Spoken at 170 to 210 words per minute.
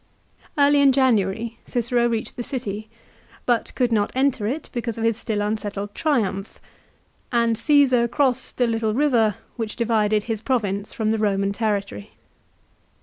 No: average, 145 wpm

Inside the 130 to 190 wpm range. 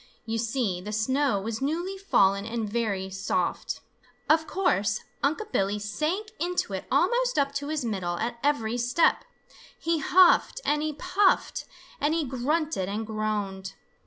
Yes: average, 150 wpm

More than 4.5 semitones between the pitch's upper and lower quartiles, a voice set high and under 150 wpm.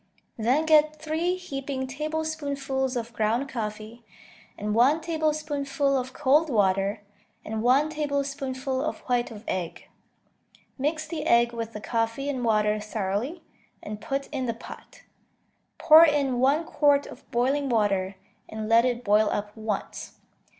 Yes: average, 4.9 semitones; very high, 260 Hz; average, 140 wpm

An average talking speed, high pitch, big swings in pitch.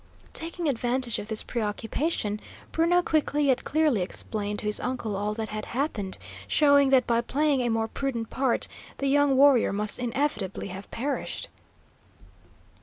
No: average, 150 wpm; high, 245 Hz; average, 5.0 semitones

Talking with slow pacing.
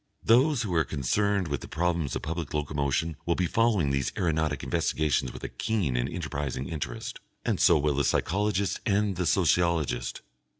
No: average, 170 wpm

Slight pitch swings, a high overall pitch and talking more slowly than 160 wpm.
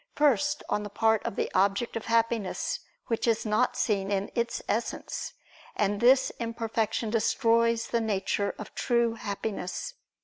Yes: narrow, 2.2 semitones; high, 225 Hz; average, 145 wpm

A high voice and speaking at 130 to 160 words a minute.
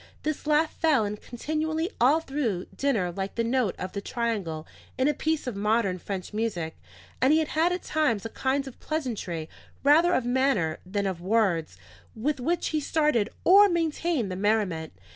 No: high, 240 Hz; average, 175 wpm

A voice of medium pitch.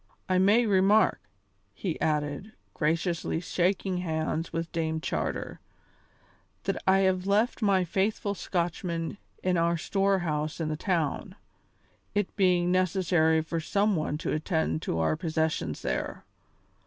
Yes: medium, 175 Hz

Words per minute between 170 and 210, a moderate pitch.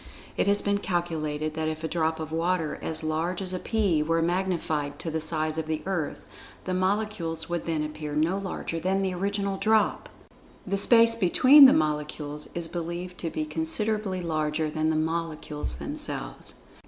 Yes: average, 175 wpm; medium, 165 Hz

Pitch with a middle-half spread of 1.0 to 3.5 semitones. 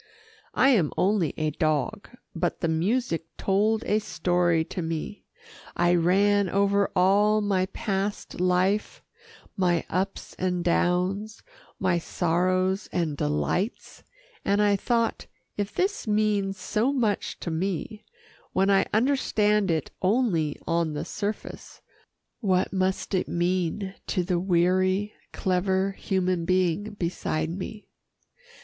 Yes: average, 2.9 semitones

